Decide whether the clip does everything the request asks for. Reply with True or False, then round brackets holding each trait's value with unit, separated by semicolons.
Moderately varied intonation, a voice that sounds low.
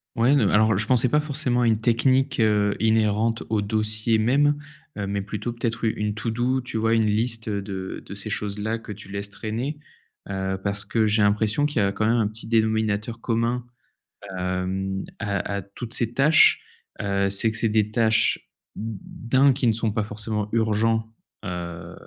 False (2.2 semitones; 110 Hz)